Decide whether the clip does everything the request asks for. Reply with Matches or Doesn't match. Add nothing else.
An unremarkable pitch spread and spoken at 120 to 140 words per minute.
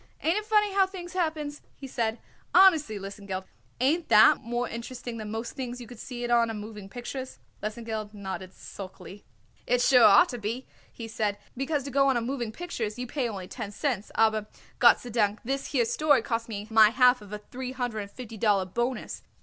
Doesn't match